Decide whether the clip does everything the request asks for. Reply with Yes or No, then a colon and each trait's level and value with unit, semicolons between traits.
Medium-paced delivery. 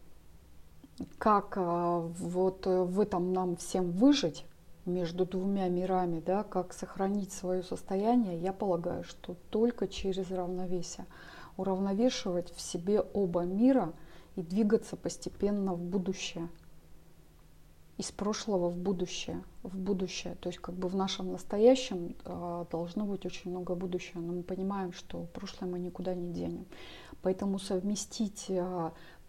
Yes: average, 125 wpm